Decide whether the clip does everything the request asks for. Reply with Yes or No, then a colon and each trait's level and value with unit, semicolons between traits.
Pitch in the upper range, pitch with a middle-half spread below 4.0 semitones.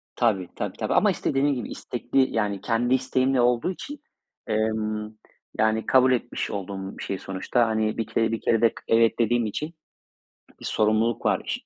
No: low, 115 Hz; narrow, 2.4 semitones